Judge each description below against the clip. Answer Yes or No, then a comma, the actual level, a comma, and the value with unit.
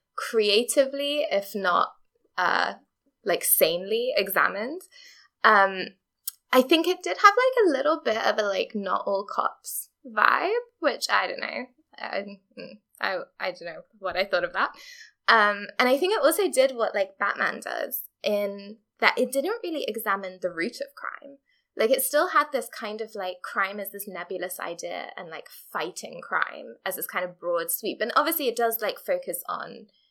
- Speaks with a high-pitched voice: Yes, very high, 255 Hz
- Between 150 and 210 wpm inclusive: Yes, average, 175 wpm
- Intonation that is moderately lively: No, wide, 8.4 semitones